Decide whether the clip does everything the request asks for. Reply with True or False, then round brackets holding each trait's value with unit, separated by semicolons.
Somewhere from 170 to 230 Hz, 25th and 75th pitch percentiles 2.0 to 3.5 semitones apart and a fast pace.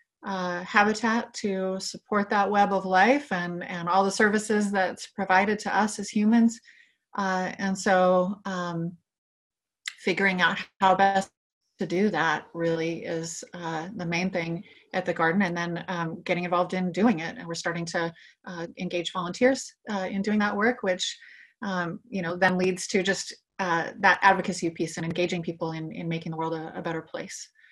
False (185 Hz; 3.0 semitones; 180 wpm)